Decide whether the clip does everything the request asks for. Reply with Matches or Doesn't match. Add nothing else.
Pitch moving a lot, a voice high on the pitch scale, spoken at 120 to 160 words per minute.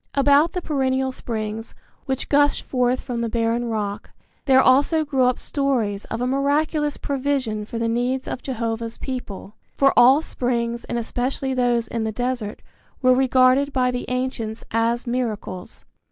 Doesn't match